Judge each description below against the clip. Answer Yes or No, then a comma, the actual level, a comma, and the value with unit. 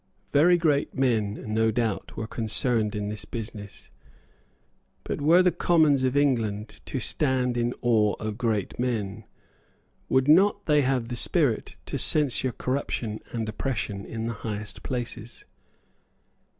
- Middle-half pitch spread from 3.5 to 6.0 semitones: Yes, average, 4.1 semitones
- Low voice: Yes, low, 120 Hz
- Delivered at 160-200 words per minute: No, slow, 135 wpm